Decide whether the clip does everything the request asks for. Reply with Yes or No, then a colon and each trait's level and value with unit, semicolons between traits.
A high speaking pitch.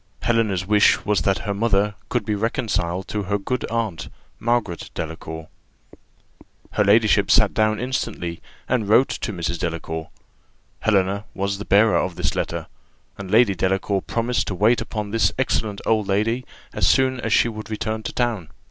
No: low, 105 Hz